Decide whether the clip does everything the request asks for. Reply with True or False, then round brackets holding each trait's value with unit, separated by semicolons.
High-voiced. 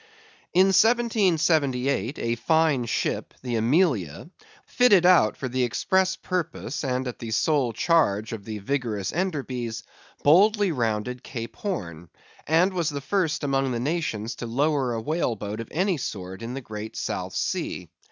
False (135 Hz)